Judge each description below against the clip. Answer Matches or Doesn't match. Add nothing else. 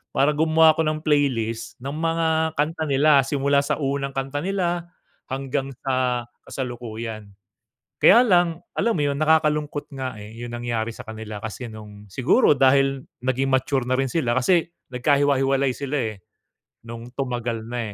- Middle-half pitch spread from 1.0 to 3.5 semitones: Doesn't match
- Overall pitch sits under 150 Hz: Matches